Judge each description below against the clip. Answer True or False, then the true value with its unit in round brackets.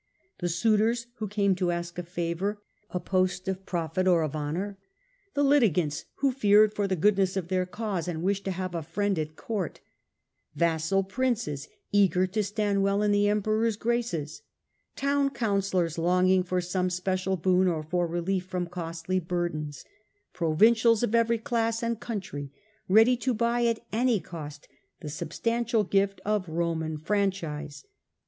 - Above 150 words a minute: True (160 wpm)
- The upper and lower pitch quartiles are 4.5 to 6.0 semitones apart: False (3.8 semitones)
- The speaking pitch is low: False (190 Hz)